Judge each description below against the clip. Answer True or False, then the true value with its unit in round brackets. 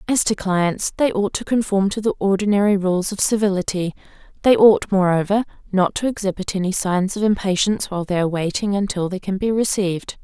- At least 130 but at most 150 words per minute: False (190 wpm)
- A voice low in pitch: False (195 Hz)